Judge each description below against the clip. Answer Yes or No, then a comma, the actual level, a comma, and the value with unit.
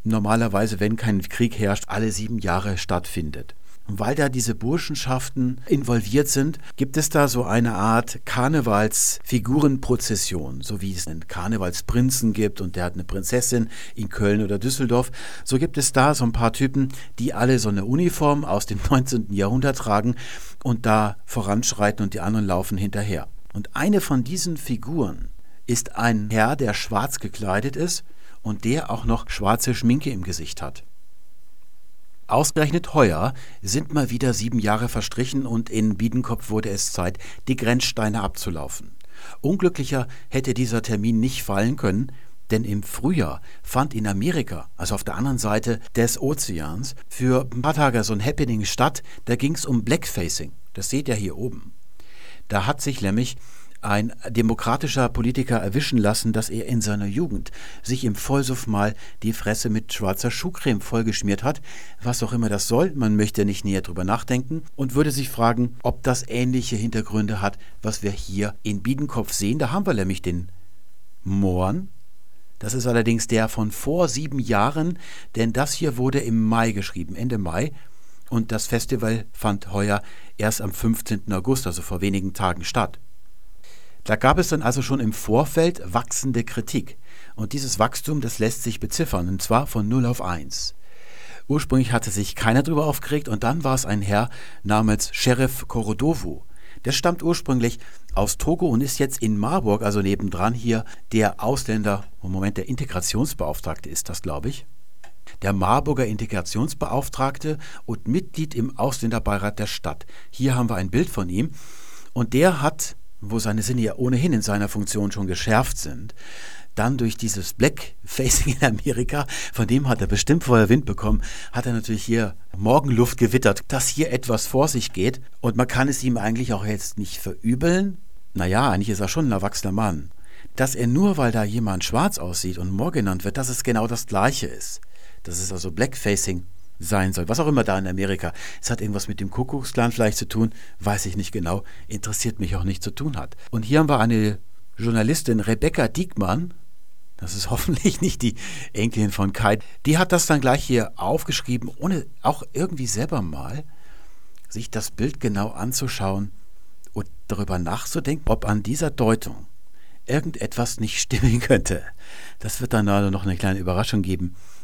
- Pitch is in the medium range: No, low, 115 Hz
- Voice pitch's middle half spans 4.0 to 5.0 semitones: Yes, average, 4.3 semitones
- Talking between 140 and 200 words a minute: Yes, average, 170 wpm